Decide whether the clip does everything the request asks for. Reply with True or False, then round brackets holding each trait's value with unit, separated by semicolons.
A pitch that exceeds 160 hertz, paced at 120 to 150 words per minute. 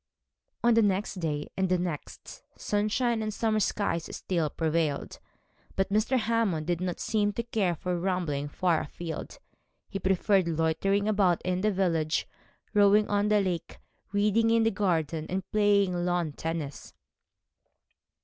True (190 Hz; 145 wpm)